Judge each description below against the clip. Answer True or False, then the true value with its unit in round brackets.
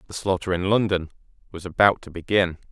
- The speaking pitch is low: True (90 Hz)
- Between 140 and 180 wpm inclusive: True (175 wpm)